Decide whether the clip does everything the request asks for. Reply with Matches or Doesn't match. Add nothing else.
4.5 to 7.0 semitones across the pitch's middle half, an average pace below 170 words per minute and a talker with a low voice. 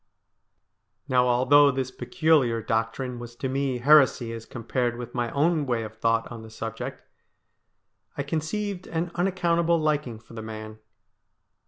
Matches